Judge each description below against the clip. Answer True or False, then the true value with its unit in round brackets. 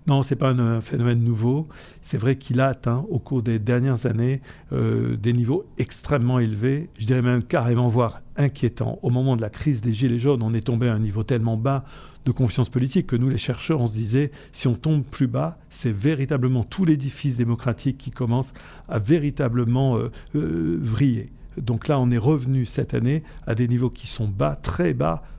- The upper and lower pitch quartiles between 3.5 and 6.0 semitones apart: False (2.6 semitones)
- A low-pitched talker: True (125 Hz)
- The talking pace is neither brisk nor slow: True (205 wpm)